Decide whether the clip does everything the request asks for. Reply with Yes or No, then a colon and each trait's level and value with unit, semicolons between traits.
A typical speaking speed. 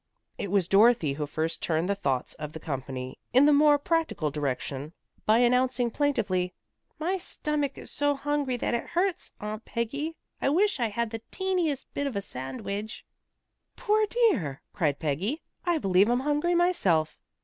Yes: average, 165 wpm